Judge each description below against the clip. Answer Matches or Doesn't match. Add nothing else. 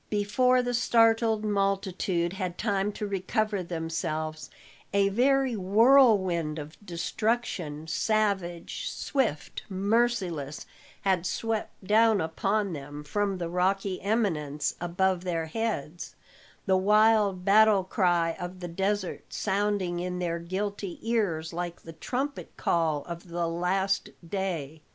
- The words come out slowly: Matches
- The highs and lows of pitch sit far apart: Doesn't match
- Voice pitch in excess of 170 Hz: Matches